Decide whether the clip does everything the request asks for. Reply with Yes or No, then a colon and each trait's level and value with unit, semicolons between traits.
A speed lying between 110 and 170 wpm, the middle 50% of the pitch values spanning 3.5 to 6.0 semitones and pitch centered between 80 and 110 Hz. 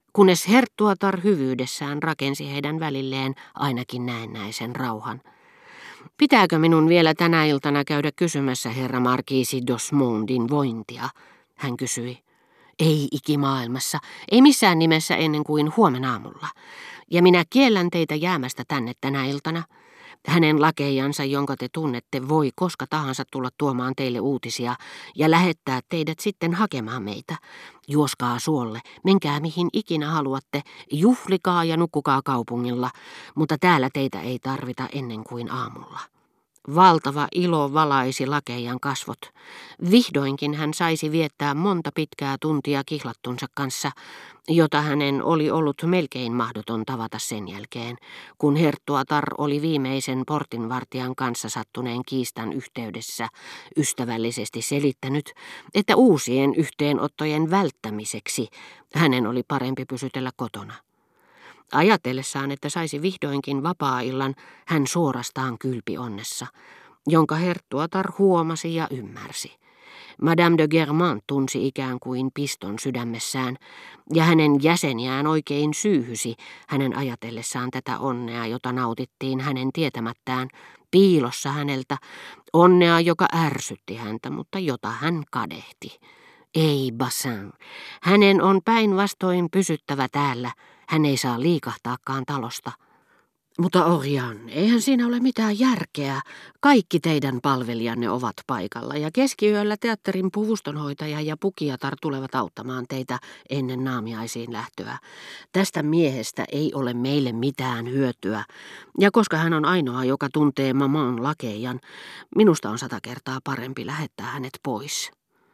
No: average, 115 wpm; average, 4.3 semitones; medium, 140 Hz